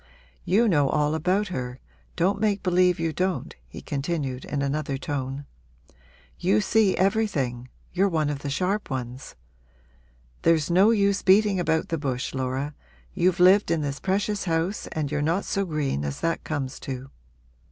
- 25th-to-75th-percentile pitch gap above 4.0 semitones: Yes, wide, 5.4 semitones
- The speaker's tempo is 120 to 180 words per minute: Yes, average, 160 wpm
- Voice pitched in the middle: Yes, medium, 160 Hz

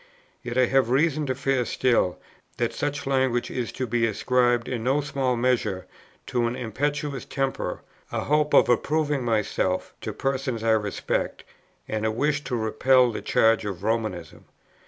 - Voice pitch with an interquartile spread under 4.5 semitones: Yes, average, 3.2 semitones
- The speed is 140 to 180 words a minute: Yes, average, 160 wpm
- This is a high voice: No, low, 125 Hz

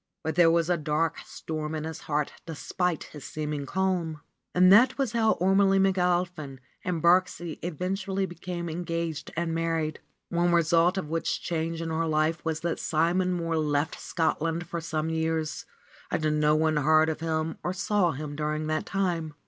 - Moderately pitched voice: Yes, medium, 165 Hz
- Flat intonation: Yes, narrow, 2.3 semitones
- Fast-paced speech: No, average, 175 wpm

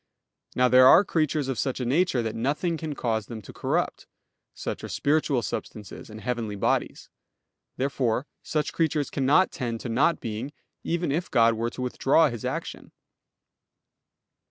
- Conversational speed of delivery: Yes, average, 155 wpm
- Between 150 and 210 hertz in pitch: No, low, 130 Hz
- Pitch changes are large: No, average, 4.6 semitones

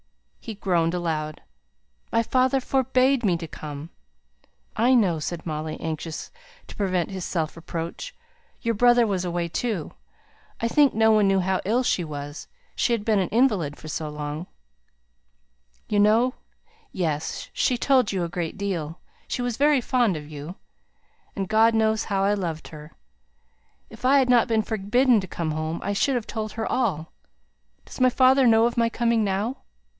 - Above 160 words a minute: Yes, average, 170 wpm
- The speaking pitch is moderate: No, high, 200 Hz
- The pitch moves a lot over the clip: Yes, wide, 6.2 semitones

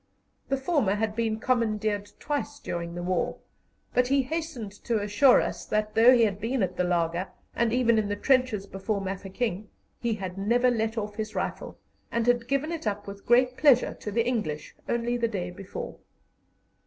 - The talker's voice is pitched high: Yes, high, 220 Hz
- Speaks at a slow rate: No, average, 185 wpm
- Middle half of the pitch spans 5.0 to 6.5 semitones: No, average, 3.6 semitones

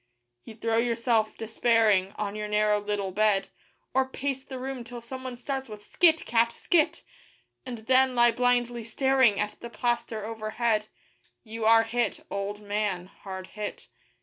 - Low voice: No, high, 230 Hz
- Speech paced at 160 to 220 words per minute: No, average, 150 wpm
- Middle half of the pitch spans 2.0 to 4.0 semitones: Yes, average, 2.8 semitones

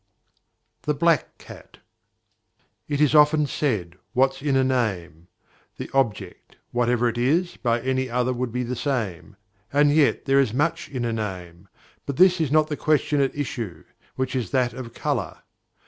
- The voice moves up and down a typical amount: Yes, average, 3.9 semitones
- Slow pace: No, average, 165 wpm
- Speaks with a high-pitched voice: No, low, 130 Hz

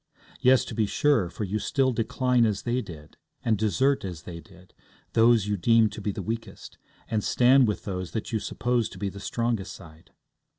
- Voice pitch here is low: Yes, low, 110 Hz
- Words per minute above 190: Yes, average, 200 wpm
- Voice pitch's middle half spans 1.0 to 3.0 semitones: No, average, 3.8 semitones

